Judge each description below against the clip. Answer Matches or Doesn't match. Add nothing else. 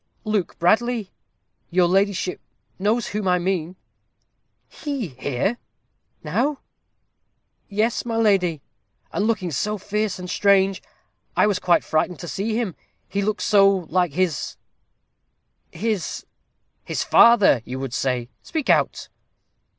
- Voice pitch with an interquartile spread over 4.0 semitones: Doesn't match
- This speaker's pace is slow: Matches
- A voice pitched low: Doesn't match